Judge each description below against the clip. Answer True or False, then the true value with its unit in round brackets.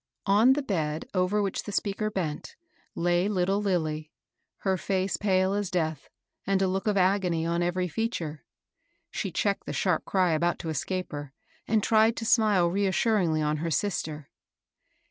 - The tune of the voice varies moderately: True (3.6 semitones)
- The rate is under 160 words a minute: False (165 wpm)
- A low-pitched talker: False (185 Hz)